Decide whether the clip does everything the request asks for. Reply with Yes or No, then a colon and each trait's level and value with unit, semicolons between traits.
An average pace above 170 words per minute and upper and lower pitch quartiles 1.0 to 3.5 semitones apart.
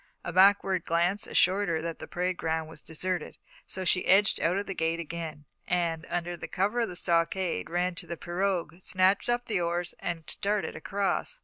Yes: average, 190 wpm; narrow, 2.5 semitones